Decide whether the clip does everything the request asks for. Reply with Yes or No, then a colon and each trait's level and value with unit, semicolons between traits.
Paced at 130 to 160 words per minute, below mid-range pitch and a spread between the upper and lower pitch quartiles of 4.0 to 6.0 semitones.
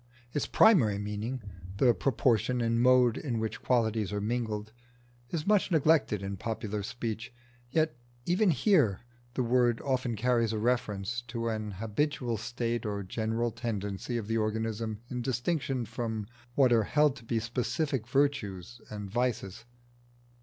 No: average, 145 wpm; low, 115 Hz; average, 2.9 semitones